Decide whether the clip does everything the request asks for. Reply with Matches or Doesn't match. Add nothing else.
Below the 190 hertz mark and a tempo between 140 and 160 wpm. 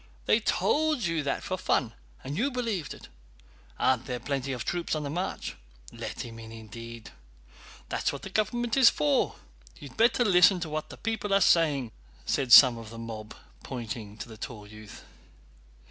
Doesn't match